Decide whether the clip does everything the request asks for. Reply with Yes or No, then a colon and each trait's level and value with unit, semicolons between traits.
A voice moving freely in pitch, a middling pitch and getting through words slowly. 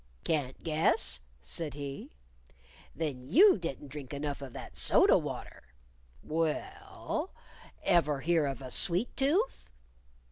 No: average, 3.8 semitones; medium, 150 Hz; slow, 115 wpm